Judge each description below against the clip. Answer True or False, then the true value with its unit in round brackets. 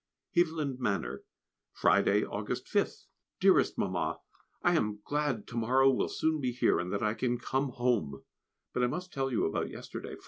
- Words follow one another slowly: False (170 wpm)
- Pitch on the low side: True (125 Hz)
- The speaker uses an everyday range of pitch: True (4.1 semitones)